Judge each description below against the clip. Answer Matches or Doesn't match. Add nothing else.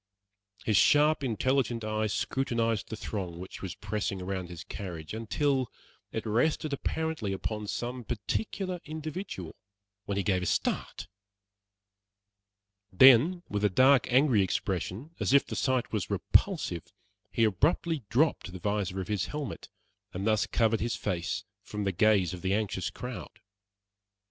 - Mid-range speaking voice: Doesn't match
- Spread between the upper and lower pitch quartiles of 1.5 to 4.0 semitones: Doesn't match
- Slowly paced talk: Doesn't match